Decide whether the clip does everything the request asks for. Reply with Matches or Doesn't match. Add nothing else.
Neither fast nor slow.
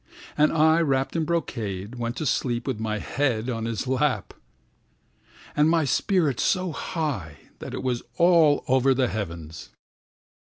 Matches